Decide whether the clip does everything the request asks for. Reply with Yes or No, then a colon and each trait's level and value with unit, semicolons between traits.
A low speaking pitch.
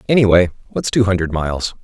Yes: very low, 95 Hz